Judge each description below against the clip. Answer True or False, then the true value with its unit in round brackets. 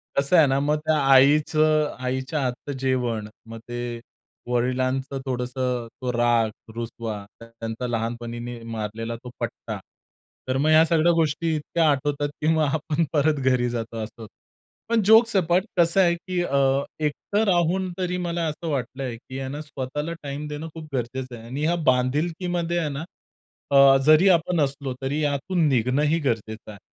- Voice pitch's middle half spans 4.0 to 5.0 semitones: True (4.4 semitones)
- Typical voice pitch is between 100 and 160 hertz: True (140 Hz)